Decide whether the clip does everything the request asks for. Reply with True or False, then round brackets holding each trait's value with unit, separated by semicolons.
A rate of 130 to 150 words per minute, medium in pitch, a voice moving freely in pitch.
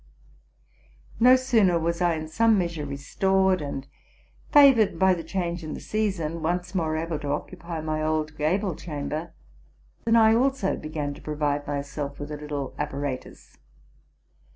False (145 wpm; 165 Hz; 4.3 semitones)